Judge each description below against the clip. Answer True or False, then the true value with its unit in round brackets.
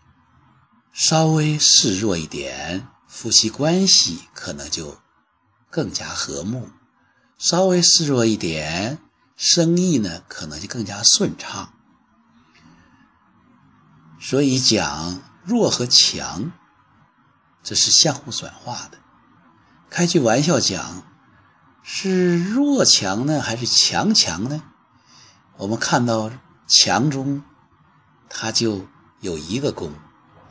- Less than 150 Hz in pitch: True (140 Hz)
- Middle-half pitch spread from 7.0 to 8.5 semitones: True (7.6 semitones)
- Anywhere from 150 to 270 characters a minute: False (140 characters per minute)